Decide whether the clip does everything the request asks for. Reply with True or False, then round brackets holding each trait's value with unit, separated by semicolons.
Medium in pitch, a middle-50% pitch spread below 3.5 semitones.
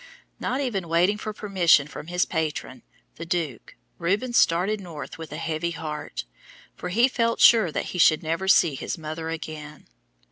False (170 Hz; 4.0 semitones)